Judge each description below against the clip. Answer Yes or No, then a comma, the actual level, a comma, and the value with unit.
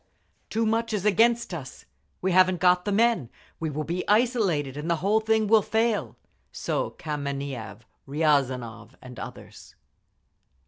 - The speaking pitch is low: No, medium, 180 Hz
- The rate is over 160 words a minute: No, average, 140 wpm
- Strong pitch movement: Yes, wide, 7.4 semitones